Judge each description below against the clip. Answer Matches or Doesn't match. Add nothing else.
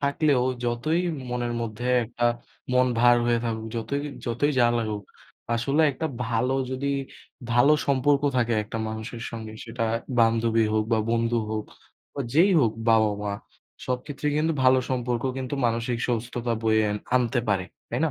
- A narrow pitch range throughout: Matches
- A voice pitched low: Matches